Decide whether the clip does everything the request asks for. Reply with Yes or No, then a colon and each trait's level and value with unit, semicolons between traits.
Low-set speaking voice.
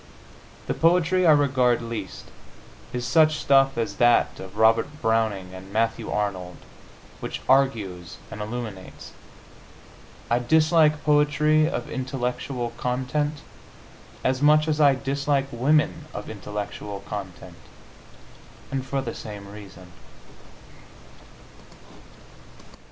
Yes: low, 125 Hz